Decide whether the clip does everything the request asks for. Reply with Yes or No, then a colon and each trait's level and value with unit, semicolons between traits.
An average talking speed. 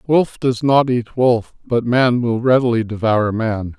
Yes: average, 175 wpm